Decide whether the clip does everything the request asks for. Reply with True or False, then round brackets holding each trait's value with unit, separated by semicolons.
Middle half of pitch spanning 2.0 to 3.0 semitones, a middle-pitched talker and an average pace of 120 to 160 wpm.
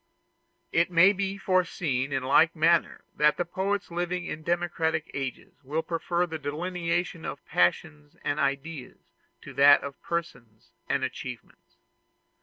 False (3.8 semitones; 160 Hz; 135 wpm)